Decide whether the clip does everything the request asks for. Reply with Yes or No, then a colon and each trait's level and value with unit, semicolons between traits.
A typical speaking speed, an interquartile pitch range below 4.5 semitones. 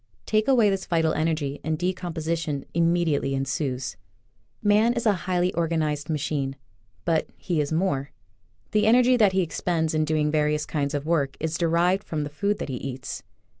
Yes: average, 175 wpm; average, 3.5 semitones